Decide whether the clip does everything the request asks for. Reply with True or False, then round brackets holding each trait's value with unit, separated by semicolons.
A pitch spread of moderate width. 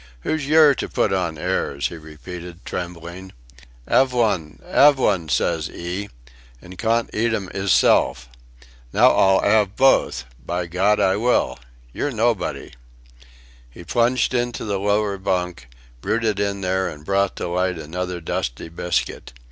True (4.1 semitones)